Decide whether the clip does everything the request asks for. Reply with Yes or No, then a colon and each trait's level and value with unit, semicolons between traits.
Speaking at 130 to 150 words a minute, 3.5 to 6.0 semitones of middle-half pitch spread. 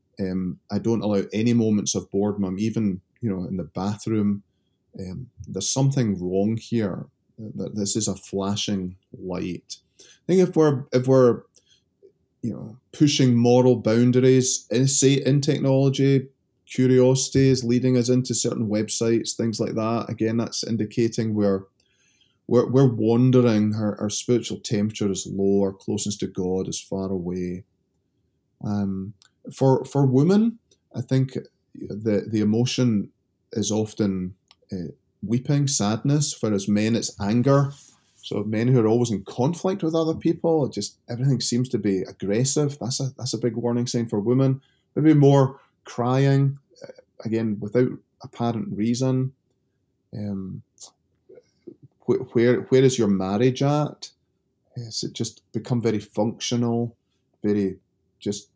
Yes: average, 140 wpm; average, 4.1 semitones